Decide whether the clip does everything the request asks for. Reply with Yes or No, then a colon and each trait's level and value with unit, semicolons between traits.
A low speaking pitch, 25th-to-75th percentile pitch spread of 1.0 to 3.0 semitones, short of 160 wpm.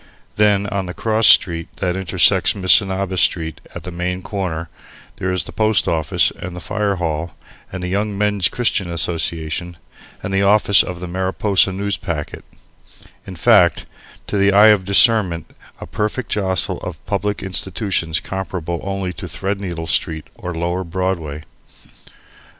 Yes: very low, 95 Hz; average, 2.7 semitones; average, 150 wpm